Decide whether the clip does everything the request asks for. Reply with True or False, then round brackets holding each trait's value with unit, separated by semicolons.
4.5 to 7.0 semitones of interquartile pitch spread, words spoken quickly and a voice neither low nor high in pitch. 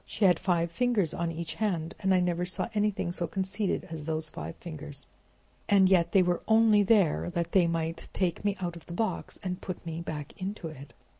False (2.9 semitones; 210 wpm; 175 Hz)